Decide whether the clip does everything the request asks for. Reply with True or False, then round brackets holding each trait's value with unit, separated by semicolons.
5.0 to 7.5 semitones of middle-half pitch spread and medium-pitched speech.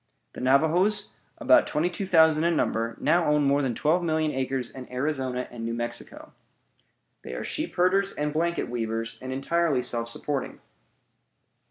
True (5.3 semitones; 150 Hz)